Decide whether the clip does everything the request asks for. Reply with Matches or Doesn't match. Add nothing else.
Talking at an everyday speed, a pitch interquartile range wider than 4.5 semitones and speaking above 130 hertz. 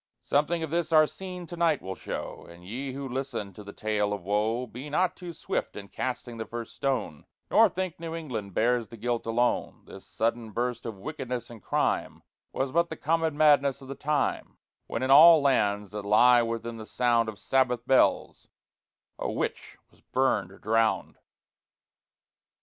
Doesn't match